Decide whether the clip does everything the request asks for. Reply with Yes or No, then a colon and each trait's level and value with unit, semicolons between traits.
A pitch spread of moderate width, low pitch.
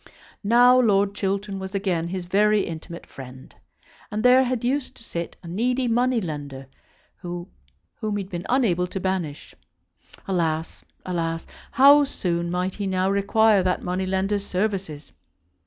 No: average, 3.8 semitones; high, 190 Hz